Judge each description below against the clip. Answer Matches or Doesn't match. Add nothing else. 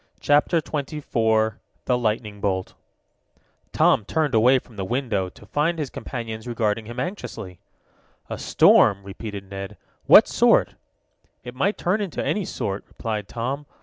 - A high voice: Doesn't match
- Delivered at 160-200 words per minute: Doesn't match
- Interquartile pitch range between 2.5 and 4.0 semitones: Doesn't match